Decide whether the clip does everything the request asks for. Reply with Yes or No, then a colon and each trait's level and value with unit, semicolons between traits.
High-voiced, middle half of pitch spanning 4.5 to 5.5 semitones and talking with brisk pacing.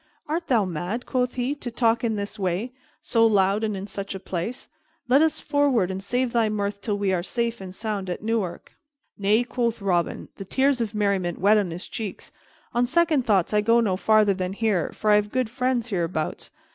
No: high, 215 Hz; average, 3.8 semitones; fast, 210 wpm